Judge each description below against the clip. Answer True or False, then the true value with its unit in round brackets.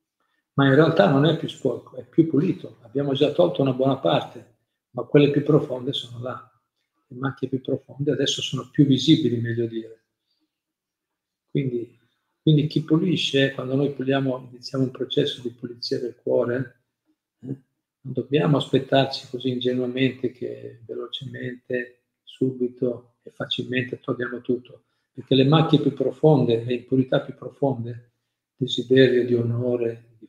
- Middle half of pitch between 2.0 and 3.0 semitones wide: True (2.5 semitones)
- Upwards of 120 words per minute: True (140 wpm)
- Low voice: True (130 Hz)